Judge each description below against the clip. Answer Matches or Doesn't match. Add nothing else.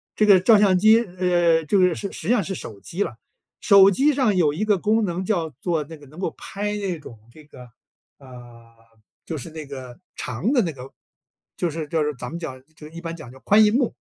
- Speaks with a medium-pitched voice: Matches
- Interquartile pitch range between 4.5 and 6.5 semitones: Matches